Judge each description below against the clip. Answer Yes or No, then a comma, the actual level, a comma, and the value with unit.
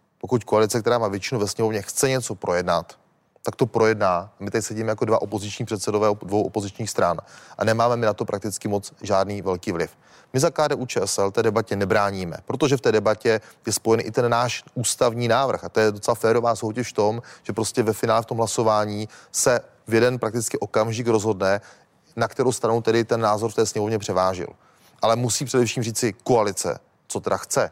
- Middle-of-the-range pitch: No, low, 110 Hz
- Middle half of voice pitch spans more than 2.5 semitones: No, narrow, 2.2 semitones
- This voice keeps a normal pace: No, fast, 195 wpm